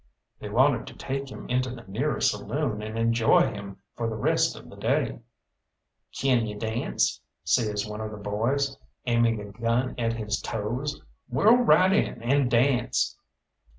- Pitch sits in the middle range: No, low, 115 Hz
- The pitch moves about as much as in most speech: Yes, average, 3.6 semitones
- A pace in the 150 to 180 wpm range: Yes, average, 160 wpm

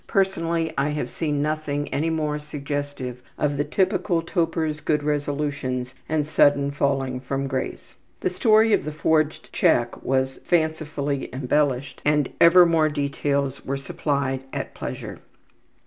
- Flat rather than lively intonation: Yes, narrow, 2.2 semitones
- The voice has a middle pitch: Yes, medium, 145 Hz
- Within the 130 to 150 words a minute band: Yes, slow, 135 wpm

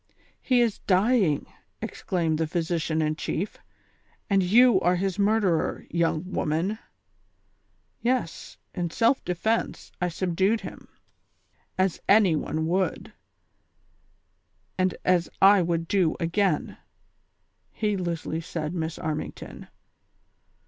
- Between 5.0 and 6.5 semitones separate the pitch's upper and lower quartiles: No, average, 3.5 semitones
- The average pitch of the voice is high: No, medium, 180 Hz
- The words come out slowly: Yes, slow, 105 wpm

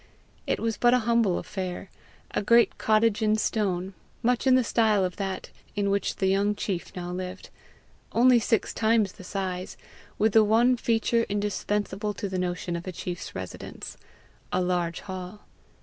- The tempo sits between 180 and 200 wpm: No, average, 165 wpm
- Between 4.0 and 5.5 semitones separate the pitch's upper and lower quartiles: No, average, 3.4 semitones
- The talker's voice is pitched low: No, high, 205 Hz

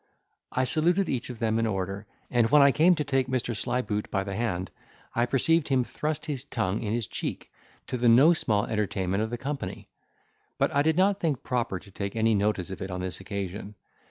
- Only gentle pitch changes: No, wide, 5.6 semitones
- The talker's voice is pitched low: Yes, low, 115 Hz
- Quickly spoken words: Yes, fast, 215 wpm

